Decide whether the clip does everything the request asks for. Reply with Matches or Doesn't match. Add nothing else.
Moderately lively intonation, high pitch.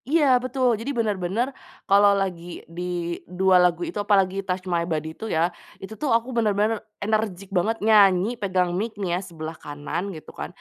Matches